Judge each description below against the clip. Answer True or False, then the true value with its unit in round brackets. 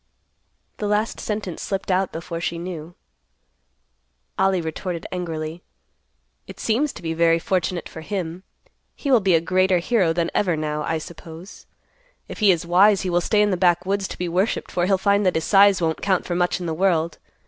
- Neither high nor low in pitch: True (180 Hz)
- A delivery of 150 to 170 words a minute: False (190 wpm)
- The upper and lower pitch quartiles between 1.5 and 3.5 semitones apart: True (2.7 semitones)